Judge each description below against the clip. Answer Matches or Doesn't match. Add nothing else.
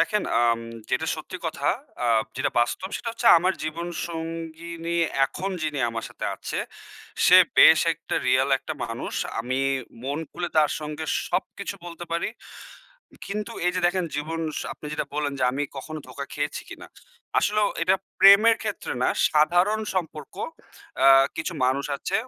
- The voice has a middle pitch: Matches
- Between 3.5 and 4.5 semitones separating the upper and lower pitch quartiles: Matches